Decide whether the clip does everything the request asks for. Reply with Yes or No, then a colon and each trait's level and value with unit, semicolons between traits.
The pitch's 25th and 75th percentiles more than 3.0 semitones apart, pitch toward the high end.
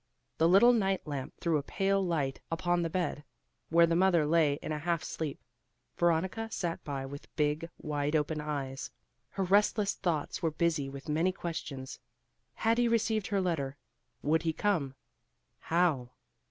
No: average, 3.9 semitones; medium, 165 Hz